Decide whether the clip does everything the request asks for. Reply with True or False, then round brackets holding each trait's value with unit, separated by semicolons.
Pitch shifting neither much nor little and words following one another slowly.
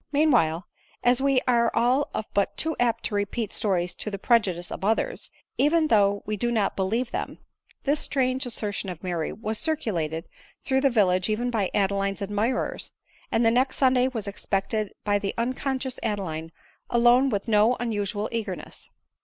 False (4.1 semitones; 170 wpm)